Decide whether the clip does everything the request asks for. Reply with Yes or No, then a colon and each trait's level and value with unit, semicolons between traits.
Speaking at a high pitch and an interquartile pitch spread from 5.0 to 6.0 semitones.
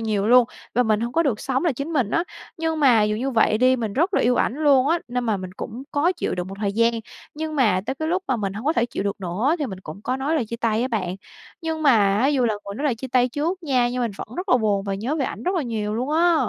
Yes: high, 245 Hz; wide, 5.5 semitones